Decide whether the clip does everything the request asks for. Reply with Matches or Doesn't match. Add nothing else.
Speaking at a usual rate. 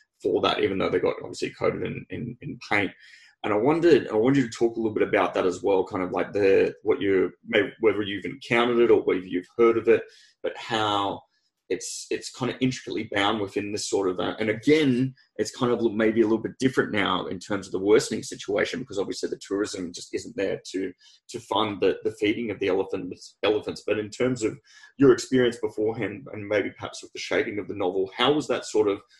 Doesn't match